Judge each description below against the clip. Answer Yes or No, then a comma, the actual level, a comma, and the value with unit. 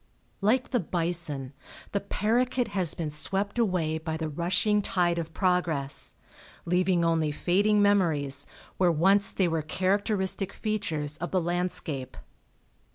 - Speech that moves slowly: Yes, slow, 130 wpm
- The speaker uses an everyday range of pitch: Yes, average, 4.0 semitones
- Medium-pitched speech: Yes, medium, 175 Hz